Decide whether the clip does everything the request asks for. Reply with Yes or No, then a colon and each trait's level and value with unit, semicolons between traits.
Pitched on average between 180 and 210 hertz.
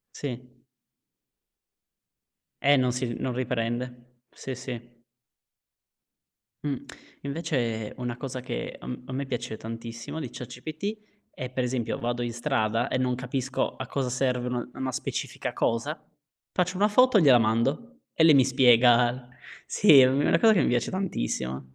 No: low, 125 Hz